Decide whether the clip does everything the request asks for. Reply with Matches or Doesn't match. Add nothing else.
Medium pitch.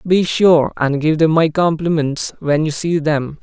Matches